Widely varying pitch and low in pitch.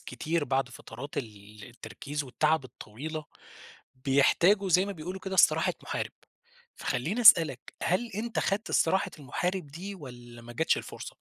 No: wide, 6.6 semitones; medium, 155 Hz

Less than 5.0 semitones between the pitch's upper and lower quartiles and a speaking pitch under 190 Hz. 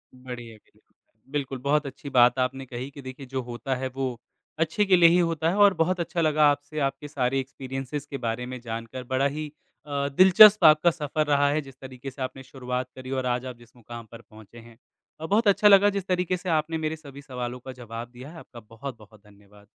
Yes: average, 3.9 semitones; low, 135 Hz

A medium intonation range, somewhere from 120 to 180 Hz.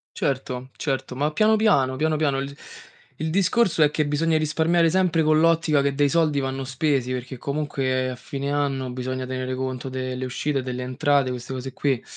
Yes: average, 3.1 semitones; medium, 140 Hz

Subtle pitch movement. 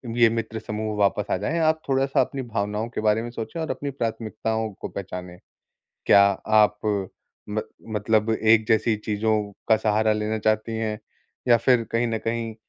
Yes: narrow, 1.4 semitones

